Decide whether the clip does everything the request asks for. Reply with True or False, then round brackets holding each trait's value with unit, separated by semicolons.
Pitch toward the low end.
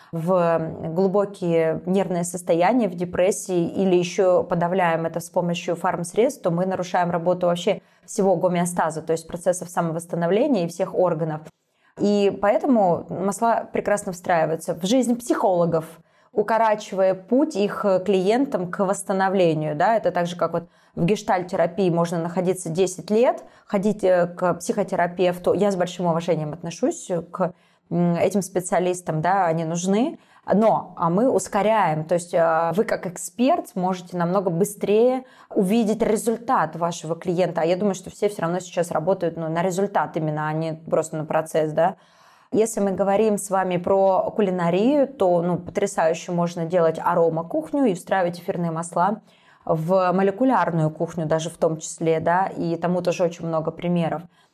False (180 Hz)